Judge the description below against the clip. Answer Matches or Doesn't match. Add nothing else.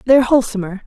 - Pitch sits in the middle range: Doesn't match